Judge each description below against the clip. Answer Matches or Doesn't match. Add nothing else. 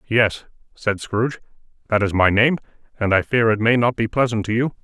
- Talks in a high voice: Doesn't match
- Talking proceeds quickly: Matches